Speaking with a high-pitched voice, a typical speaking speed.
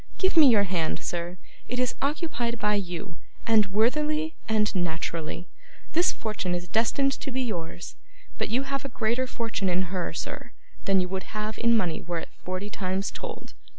Yes: high, 210 Hz; average, 180 wpm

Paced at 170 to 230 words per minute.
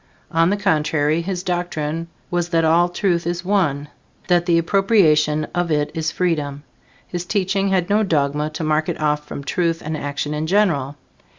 Yes: average, 175 wpm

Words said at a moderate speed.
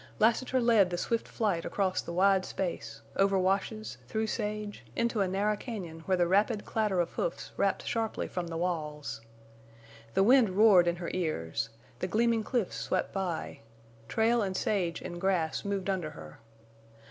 Yes: average, 165 wpm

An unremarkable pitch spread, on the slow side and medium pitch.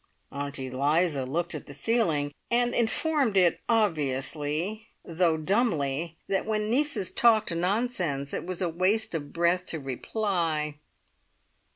No: wide, 6.5 semitones; slow, 125 wpm; medium, 170 Hz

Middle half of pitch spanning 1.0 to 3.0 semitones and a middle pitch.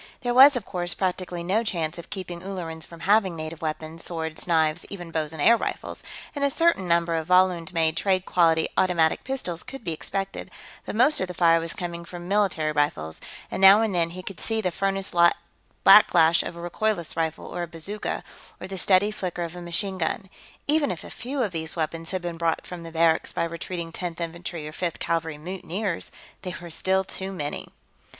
Yes: average, 2.7 semitones; medium, 175 Hz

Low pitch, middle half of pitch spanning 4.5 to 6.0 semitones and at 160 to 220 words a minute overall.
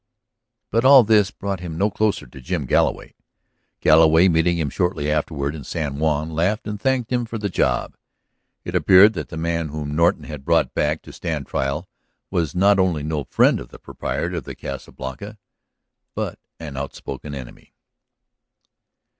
Yes: very low, 80 Hz; average, 4.9 semitones; average, 170 wpm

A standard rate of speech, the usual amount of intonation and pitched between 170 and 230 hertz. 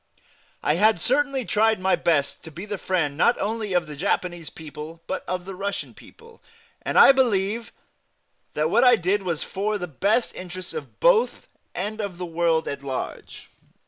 Yes: average, 175 wpm; average, 4.6 semitones; high, 190 Hz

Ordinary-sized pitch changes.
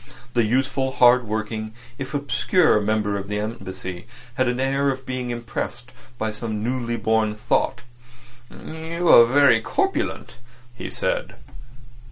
Yes: average, 3.5 semitones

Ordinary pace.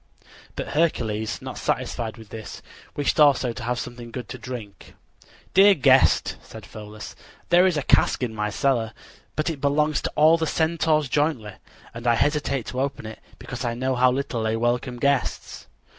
Yes: average, 175 wpm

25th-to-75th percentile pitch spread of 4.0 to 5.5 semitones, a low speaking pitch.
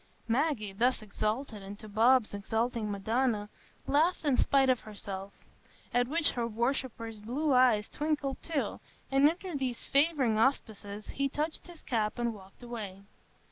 No: average, 4.5 semitones; high, 240 Hz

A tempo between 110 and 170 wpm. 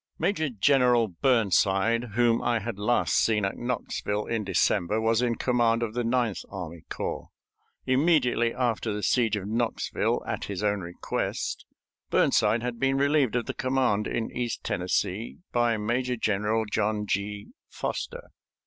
Yes: average, 150 wpm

